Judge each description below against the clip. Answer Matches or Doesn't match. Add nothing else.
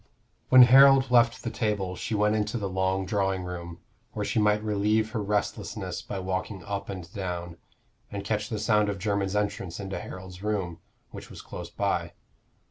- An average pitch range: Doesn't match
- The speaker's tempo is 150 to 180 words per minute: Matches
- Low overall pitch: Matches